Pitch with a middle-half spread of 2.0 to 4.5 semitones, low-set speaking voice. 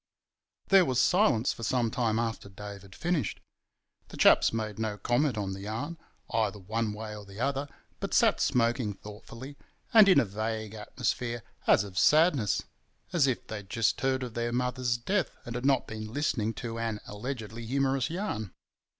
Yes: average, 3.7 semitones; low, 115 Hz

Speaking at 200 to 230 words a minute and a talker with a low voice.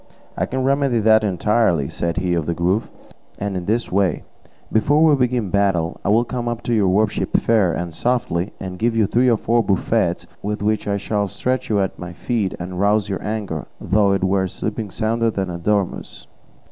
Yes: fast, 205 wpm; low, 105 Hz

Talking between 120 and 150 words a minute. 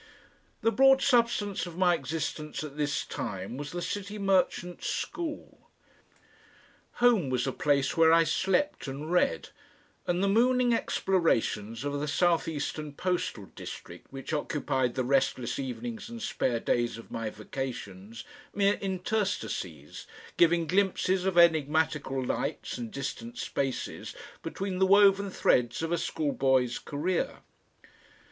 Yes: slow, 135 wpm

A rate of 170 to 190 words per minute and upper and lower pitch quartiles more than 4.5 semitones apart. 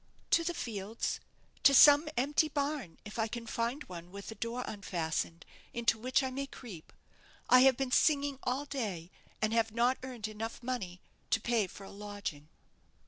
Yes: average, 175 wpm; average, 4.9 semitones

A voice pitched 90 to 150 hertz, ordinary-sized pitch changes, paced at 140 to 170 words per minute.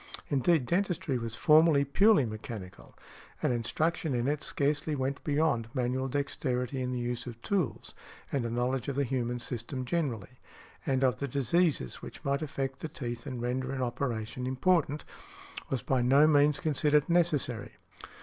Yes: low, 135 Hz; average, 3.3 semitones; average, 160 wpm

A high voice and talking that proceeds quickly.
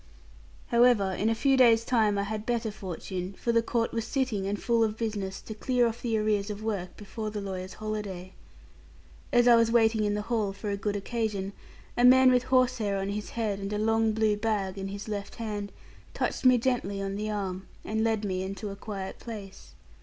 Yes: high, 215 Hz; fast, 210 wpm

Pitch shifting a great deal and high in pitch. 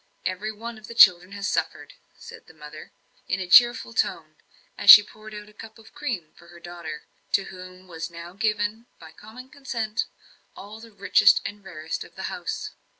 No: average, 4.0 semitones; high, 205 Hz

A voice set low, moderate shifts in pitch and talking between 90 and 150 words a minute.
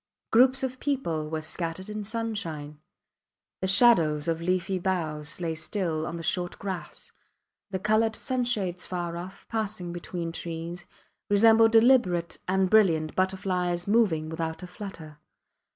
No: medium, 180 Hz; average, 4.3 semitones; slow, 135 wpm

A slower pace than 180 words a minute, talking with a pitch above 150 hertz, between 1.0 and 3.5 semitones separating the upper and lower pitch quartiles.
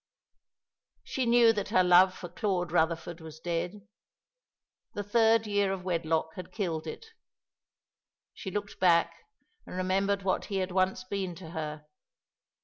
Yes: average, 140 wpm; medium, 185 Hz; average, 3.1 semitones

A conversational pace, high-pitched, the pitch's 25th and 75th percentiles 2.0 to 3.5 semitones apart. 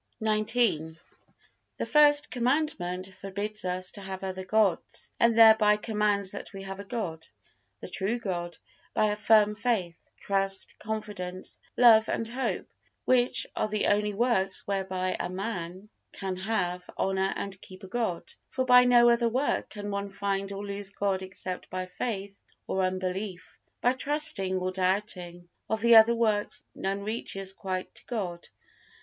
Yes: average, 155 wpm; high, 200 Hz; average, 2.9 semitones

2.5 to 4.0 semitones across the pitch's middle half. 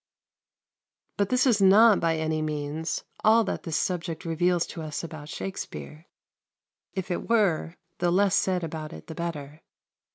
Yes: average, 3.5 semitones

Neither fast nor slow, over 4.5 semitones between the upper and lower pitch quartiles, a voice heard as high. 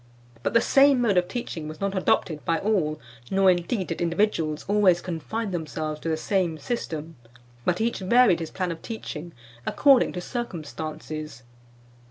No: average, 160 wpm; average, 4.9 semitones; medium, 175 Hz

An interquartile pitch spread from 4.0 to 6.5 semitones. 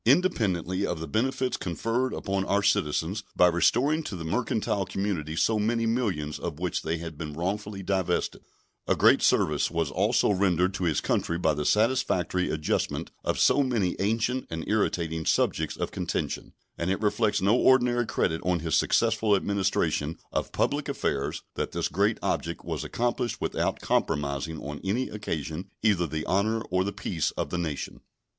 Yes: average, 5.1 semitones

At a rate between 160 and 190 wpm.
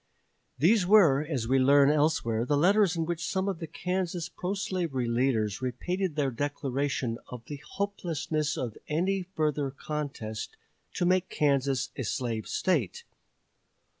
No: average, 140 wpm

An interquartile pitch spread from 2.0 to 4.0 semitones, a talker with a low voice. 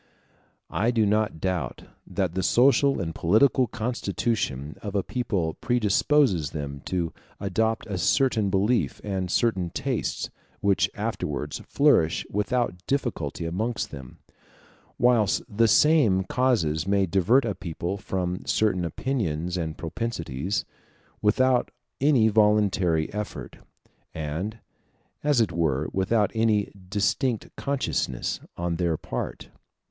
No: average, 5.3 semitones; low, 100 Hz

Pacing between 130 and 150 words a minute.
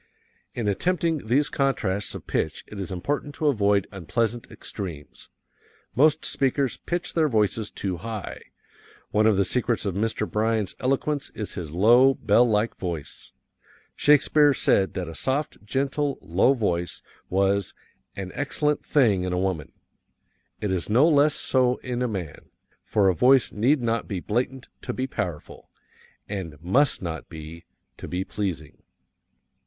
Yes: average, 145 wpm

